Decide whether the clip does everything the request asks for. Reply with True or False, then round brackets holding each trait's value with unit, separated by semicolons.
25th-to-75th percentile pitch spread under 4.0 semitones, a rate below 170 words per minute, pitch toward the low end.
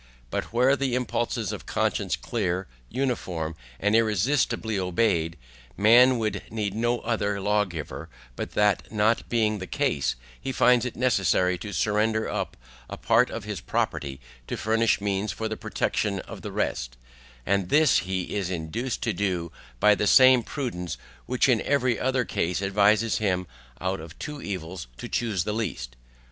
False (4.3 semitones; 160 wpm; 105 Hz)